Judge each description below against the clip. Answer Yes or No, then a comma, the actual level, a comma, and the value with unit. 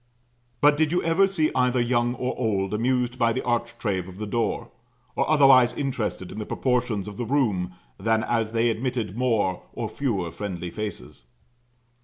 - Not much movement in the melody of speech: No, average, 3.6 semitones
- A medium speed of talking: Yes, average, 170 wpm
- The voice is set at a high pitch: No, low, 120 Hz